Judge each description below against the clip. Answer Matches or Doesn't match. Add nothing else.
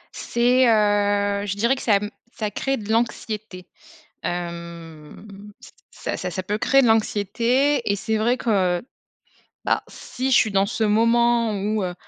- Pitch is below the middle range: Doesn't match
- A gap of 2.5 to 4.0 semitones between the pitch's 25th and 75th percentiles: Matches